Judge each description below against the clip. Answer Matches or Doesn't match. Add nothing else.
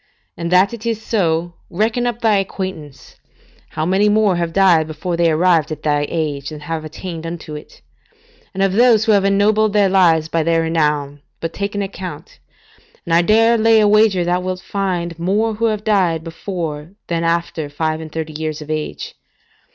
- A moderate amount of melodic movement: Matches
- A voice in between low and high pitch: Matches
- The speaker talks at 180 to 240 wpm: Matches